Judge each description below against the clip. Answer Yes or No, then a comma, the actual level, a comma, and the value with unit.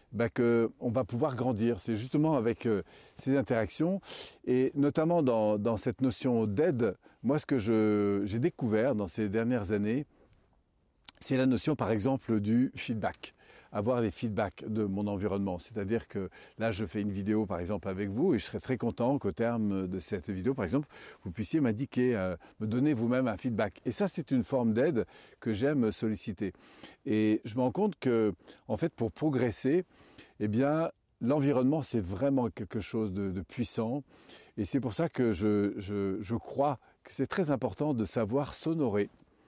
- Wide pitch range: No, average, 4.0 semitones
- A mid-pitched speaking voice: No, low, 115 Hz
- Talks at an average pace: Yes, average, 180 wpm